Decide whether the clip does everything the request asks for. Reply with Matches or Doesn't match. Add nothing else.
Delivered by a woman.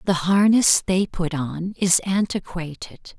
Matches